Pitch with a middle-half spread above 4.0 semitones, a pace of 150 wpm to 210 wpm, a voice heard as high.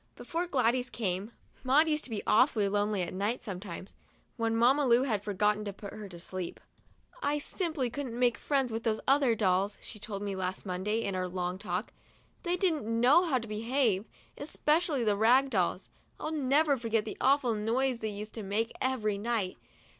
Yes: average, 4.6 semitones; average, 185 wpm; high, 225 Hz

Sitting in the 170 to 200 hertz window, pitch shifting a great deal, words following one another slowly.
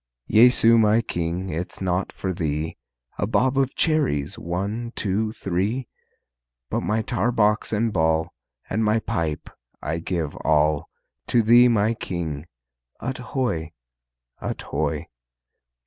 No: low, 100 Hz; wide, 5.9 semitones; slow, 130 wpm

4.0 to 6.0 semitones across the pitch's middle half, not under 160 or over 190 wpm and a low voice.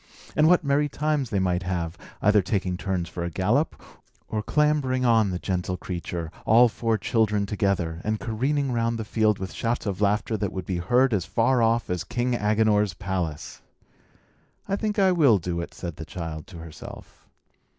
Yes: average, 5.1 semitones; average, 180 wpm; low, 105 Hz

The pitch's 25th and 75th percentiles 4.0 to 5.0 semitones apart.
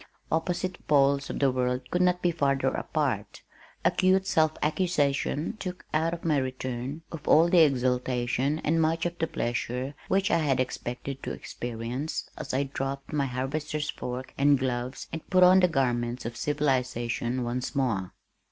Yes: average, 4.3 semitones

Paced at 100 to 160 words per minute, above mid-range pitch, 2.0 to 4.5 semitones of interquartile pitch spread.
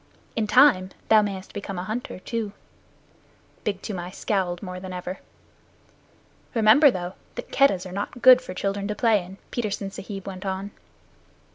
Yes: average, 155 wpm; high, 200 Hz; average, 2.7 semitones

